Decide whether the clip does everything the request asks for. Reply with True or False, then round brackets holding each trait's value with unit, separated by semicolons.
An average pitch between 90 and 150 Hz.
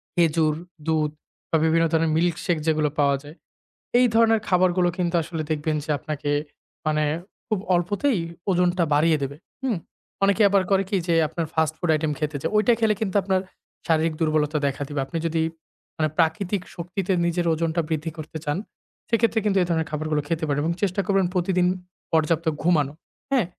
False (165 Hz)